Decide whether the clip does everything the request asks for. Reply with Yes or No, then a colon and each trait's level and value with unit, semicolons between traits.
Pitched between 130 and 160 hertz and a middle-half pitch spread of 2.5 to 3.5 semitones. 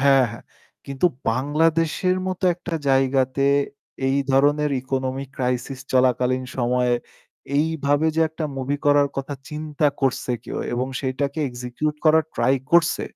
Yes: low, 135 Hz; average, 2.8 semitones